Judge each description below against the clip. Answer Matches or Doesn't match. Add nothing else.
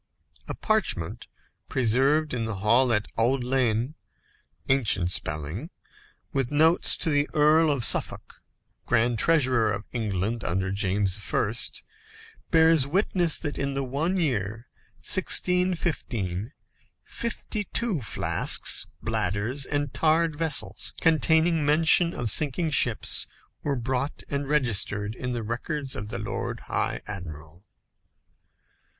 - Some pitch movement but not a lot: Doesn't match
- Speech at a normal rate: Doesn't match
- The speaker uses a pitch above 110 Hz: Matches